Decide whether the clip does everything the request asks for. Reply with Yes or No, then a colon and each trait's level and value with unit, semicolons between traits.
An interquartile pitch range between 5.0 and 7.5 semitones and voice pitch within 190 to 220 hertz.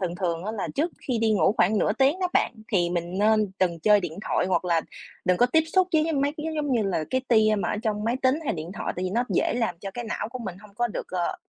Yes: wide, 5.4 semitones; high, 210 Hz